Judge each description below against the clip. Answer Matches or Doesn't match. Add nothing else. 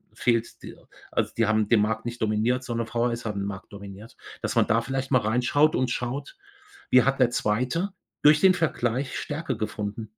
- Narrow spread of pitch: Doesn't match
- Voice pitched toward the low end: Matches